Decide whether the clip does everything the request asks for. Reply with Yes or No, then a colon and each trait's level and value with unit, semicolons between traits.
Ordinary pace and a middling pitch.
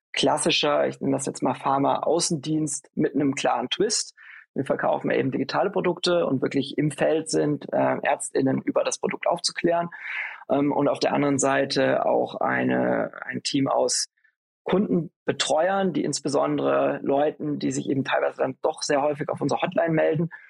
Yes: average, 160 wpm; medium, 145 Hz